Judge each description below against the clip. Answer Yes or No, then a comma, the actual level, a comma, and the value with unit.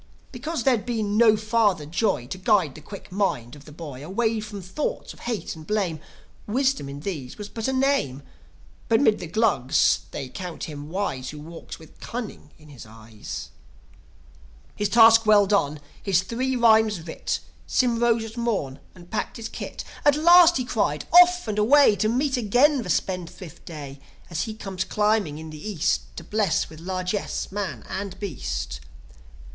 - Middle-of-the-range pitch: No, high, 200 Hz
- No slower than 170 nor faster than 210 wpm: Yes, average, 175 wpm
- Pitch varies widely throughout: Yes, wide, 6.7 semitones